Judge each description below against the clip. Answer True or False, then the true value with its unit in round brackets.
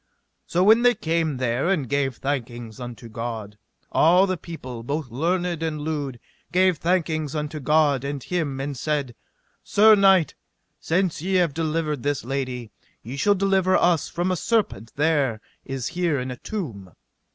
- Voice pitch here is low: False (150 Hz)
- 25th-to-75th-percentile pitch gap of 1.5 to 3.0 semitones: False (5.4 semitones)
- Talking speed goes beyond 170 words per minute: False (160 wpm)